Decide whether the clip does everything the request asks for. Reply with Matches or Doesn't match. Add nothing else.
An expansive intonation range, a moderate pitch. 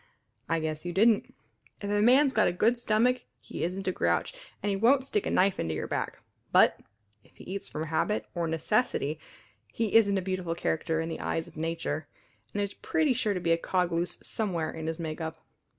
Doesn't match